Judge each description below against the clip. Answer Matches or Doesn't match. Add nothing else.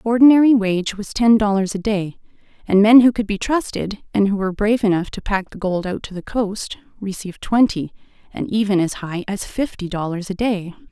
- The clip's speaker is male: Doesn't match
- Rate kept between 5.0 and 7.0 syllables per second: Matches